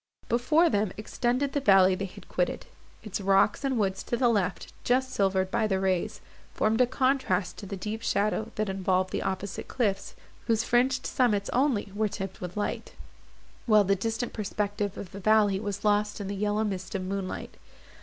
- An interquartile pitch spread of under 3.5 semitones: Yes, average, 3.1 semitones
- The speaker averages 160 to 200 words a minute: Yes, average, 185 wpm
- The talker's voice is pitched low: No, high, 205 Hz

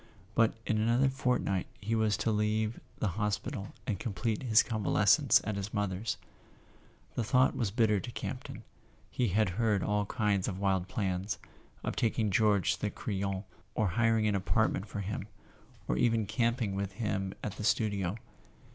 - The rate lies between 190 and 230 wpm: No, average, 160 wpm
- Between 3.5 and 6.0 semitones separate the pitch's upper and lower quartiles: No, narrow, 2.5 semitones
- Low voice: Yes, low, 105 Hz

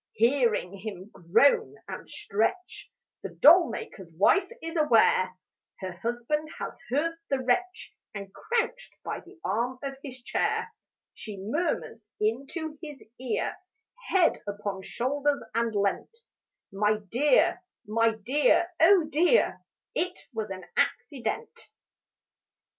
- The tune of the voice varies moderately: No, wide, 7.0 semitones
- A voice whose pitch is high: Yes, very high, 255 Hz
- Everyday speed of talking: No, slow, 115 wpm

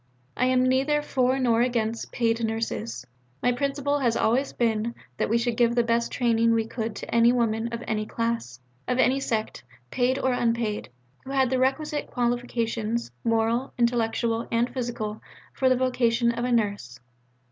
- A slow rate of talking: No, average, 170 wpm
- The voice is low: No, high, 235 Hz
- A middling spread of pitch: No, narrow, 1.9 semitones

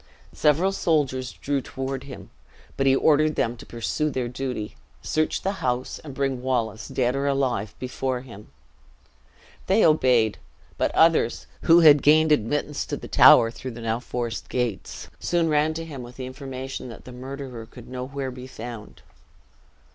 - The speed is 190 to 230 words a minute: No, average, 160 wpm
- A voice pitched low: Yes, low, 130 Hz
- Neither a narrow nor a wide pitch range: Yes, average, 3.2 semitones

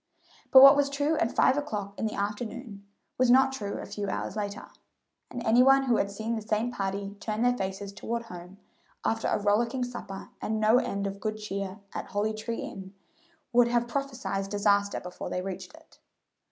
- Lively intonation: No, average, 3.5 semitones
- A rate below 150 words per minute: No, average, 195 wpm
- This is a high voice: Yes, high, 215 Hz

